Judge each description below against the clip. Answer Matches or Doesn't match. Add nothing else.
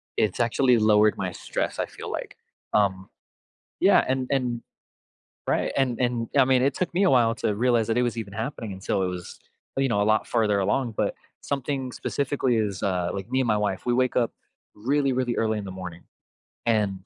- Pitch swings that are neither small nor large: Matches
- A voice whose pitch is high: Doesn't match